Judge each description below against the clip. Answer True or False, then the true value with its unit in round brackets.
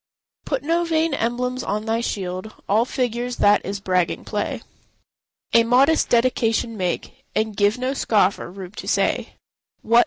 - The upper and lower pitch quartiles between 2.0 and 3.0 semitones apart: False (3.8 semitones)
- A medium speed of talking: True (145 wpm)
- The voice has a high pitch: True (230 Hz)